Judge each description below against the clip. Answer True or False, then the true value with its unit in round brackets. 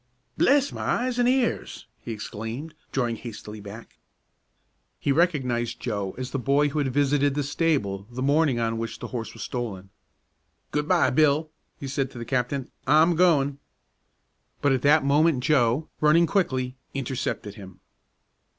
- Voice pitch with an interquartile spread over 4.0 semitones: True (4.4 semitones)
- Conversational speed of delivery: True (155 wpm)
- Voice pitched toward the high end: False (135 Hz)